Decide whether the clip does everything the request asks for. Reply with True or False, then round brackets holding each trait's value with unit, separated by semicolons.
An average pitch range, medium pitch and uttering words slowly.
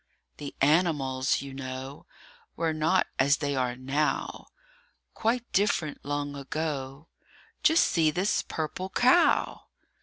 True (3.7 semitones; 145 Hz; 115 wpm)